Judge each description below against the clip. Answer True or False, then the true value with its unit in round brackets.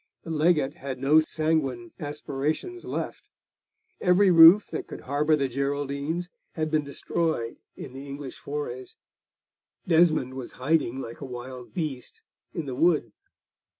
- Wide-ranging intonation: False (3.3 semitones)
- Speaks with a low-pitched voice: False (145 Hz)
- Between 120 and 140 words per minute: True (135 wpm)